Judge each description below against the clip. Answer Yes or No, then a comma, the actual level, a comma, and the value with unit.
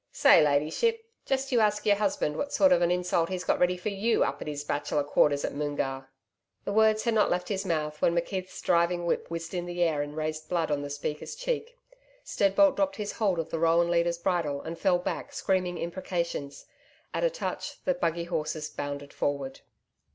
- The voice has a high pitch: No, medium, 170 Hz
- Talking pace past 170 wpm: Yes, fast, 205 wpm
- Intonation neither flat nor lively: Yes, average, 4.9 semitones